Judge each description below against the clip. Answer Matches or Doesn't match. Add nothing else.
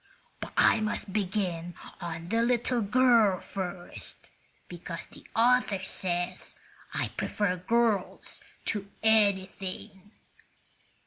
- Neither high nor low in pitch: Doesn't match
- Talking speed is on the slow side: Matches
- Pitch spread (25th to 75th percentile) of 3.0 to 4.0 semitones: Matches